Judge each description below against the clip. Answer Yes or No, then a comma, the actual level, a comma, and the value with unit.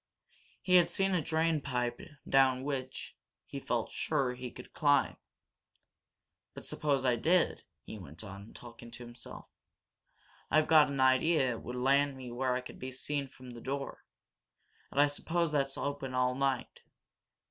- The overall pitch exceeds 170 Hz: No, low, 135 Hz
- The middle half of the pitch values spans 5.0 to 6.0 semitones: No, average, 2.7 semitones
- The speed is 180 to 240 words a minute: No, average, 160 wpm